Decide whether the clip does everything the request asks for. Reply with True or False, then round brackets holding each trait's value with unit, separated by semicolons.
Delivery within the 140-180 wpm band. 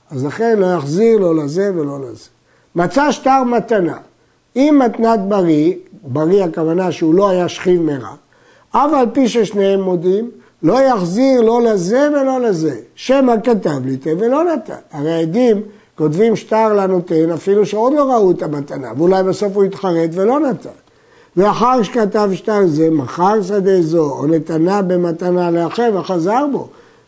True (145 wpm)